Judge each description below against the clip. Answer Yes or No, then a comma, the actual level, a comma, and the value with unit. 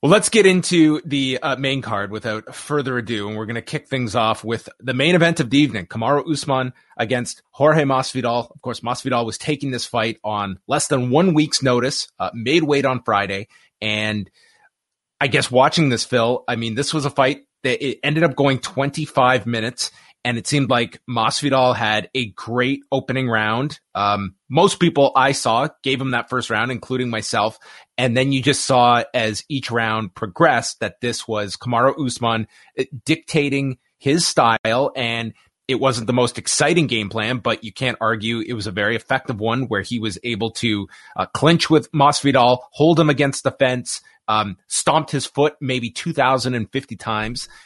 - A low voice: Yes, low, 125 Hz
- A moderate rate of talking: Yes, average, 185 wpm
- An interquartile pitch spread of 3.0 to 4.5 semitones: Yes, average, 3.8 semitones